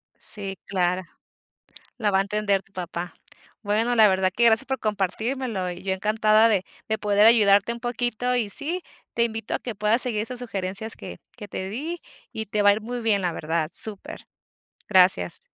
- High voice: Yes, high, 210 Hz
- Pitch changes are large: No, average, 3.4 semitones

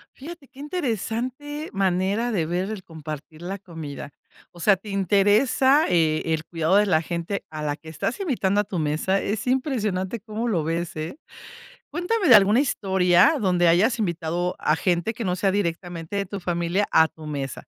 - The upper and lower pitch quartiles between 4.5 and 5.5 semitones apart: Yes, average, 5.0 semitones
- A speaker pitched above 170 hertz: Yes, high, 190 Hz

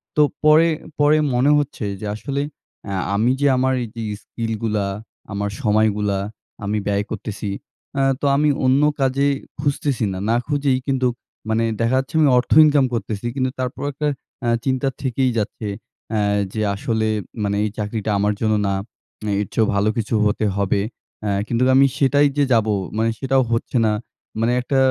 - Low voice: Yes, low, 115 Hz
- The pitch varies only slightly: No, average, 4.2 semitones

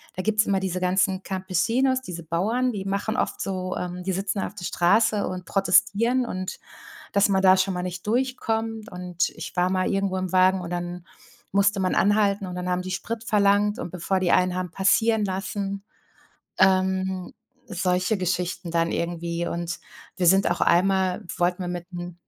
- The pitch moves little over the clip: Yes, narrow, 1.9 semitones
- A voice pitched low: No, high, 190 Hz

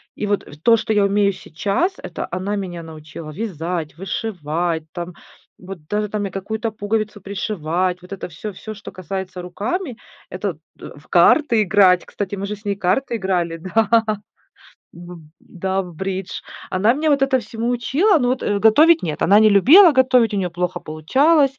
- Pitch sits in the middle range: No, high, 200 Hz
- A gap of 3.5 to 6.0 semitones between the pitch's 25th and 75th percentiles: Yes, average, 3.9 semitones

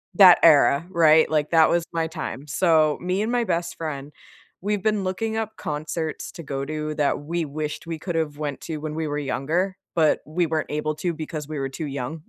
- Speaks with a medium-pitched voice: Yes, medium, 160 Hz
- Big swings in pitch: No, narrow, 2.5 semitones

